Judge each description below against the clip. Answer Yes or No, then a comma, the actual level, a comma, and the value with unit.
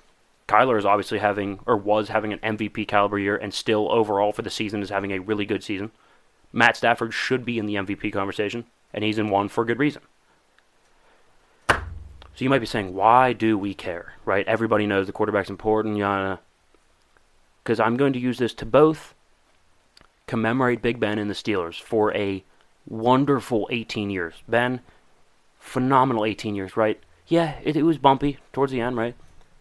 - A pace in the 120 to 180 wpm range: Yes, average, 175 wpm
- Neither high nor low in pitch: No, low, 110 Hz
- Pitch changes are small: No, average, 3.2 semitones